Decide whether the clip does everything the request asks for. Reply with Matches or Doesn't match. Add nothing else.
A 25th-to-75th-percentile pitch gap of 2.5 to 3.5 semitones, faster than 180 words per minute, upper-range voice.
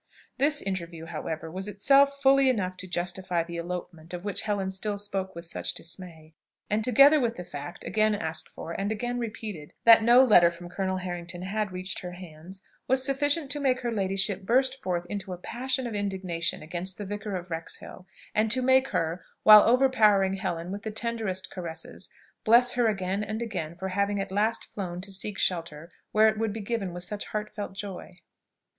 Doesn't match